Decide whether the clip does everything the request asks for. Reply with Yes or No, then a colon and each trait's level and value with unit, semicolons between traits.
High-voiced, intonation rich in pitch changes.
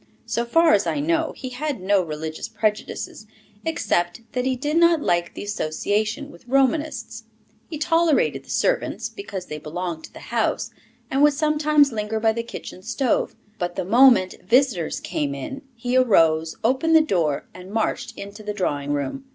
Yes: high, 225 Hz; wide, 7.7 semitones